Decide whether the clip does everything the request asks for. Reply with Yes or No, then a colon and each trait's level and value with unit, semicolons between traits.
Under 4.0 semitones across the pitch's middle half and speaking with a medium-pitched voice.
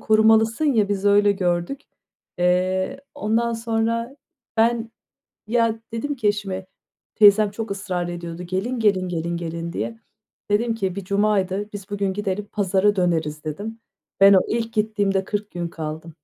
No: average, 3.3 semitones; high, 205 Hz